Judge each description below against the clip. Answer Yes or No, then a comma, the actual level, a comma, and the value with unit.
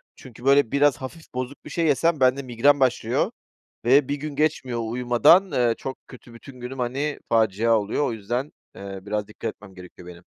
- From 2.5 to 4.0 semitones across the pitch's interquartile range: Yes, average, 3.7 semitones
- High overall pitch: No, low, 125 Hz